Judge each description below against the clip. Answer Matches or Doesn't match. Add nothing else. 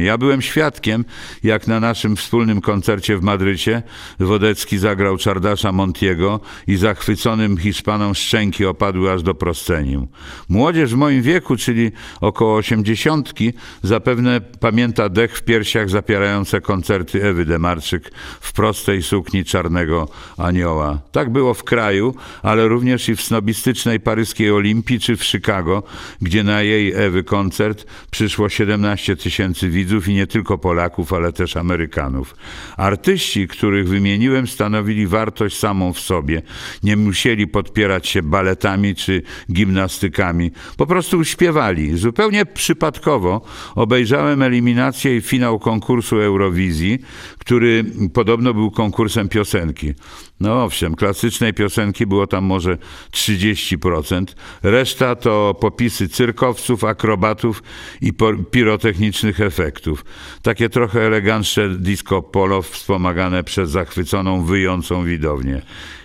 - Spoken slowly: Doesn't match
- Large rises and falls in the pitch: Doesn't match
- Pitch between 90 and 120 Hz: Matches